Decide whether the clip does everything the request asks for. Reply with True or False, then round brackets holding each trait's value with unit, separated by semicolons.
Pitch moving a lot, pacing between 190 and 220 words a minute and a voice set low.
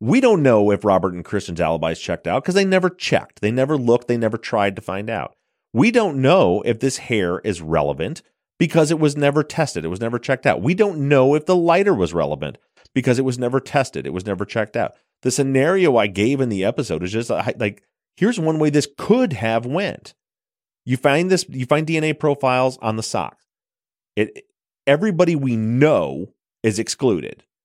True (6.1 semitones; 200 wpm; 130 Hz)